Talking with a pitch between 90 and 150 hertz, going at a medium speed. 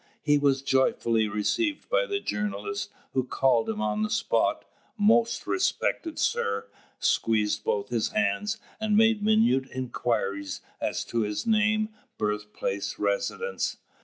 No: low, 135 Hz; slow, 130 wpm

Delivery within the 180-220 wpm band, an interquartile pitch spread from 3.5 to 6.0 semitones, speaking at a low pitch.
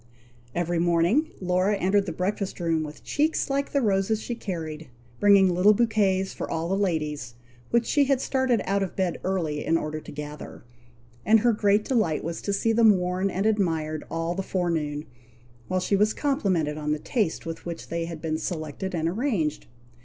No: average, 185 wpm; average, 4.3 semitones; medium, 185 Hz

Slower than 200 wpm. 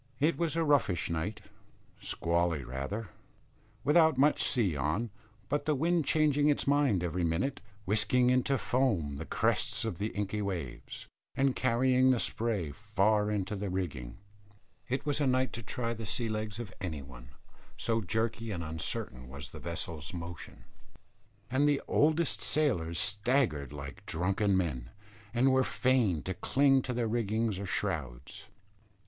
Yes: average, 150 wpm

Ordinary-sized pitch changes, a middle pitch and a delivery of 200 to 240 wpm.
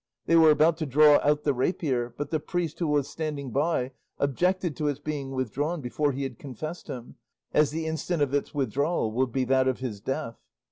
Yes: average, 3.1 semitones; medium, 145 Hz; fast, 205 wpm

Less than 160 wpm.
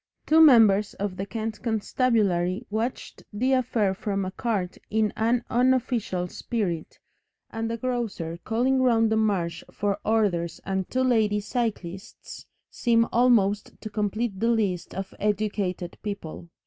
Yes: slow, 135 wpm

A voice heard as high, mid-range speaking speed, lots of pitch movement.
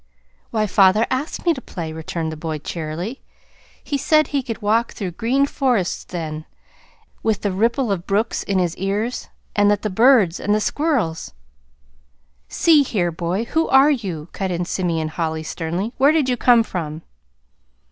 Yes: high, 200 Hz; average, 170 wpm; wide, 6.7 semitones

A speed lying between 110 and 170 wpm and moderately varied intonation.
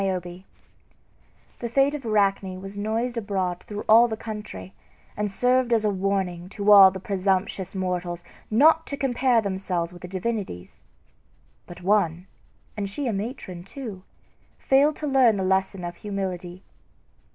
Yes: average, 145 wpm; average, 3.6 semitones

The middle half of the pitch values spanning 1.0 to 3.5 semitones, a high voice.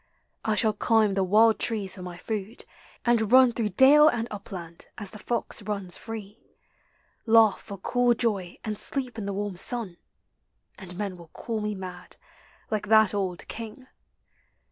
Yes: average, 2.9 semitones; high, 210 Hz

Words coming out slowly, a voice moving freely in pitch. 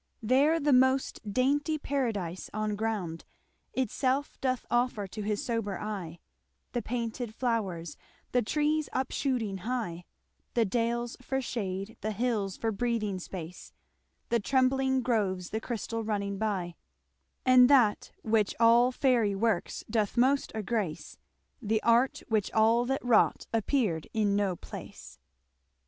No: slow, 130 wpm; average, 3.7 semitones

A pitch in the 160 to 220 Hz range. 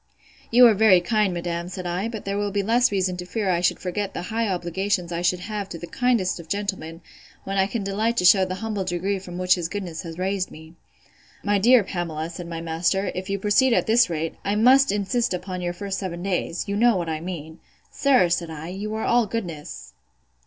Yes: high, 190 Hz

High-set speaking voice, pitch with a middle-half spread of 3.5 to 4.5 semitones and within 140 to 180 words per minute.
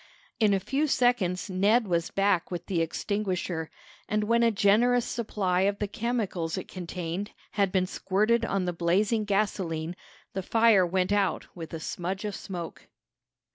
No: high, 195 Hz; average, 3.1 semitones; average, 160 wpm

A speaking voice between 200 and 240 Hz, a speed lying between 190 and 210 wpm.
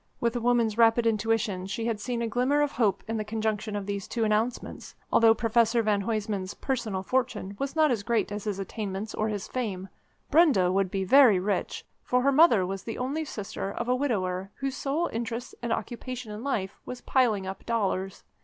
Yes: high, 225 Hz; average, 200 wpm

